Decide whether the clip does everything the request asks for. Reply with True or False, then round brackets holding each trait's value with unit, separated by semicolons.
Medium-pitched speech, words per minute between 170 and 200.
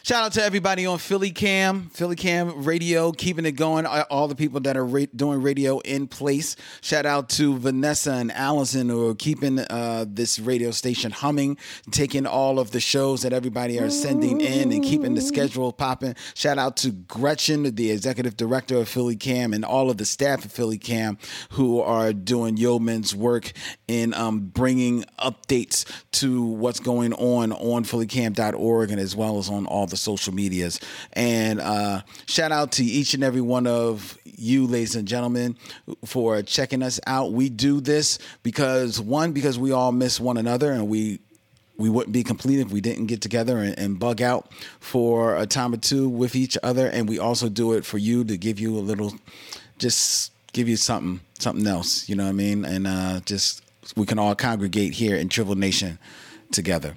False (120 Hz; 190 wpm)